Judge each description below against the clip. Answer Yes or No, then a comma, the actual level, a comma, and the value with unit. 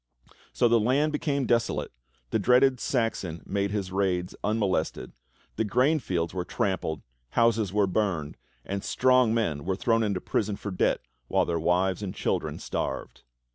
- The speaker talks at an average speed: Yes, average, 155 wpm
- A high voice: No, low, 100 Hz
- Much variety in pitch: No, average, 4.2 semitones